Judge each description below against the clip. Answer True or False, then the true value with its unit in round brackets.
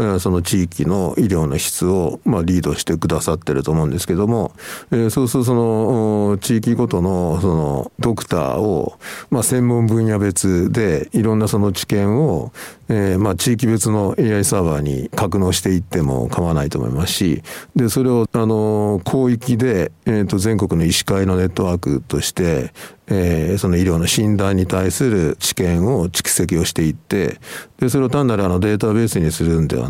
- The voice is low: True (100 Hz)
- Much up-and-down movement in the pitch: False (4.2 semitones)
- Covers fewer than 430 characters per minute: True (340 characters per minute)